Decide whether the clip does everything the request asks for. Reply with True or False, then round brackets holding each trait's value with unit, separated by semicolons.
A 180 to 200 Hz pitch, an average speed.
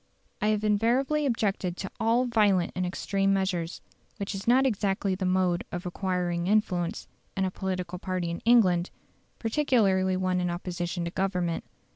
True (190 Hz; 155 wpm)